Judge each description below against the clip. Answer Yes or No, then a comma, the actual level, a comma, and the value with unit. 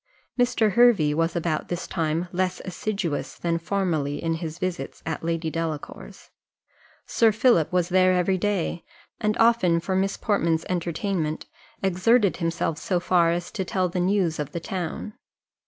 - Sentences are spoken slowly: No, average, 155 wpm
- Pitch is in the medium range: Yes, medium, 175 Hz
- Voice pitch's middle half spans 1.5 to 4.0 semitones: Yes, average, 2.8 semitones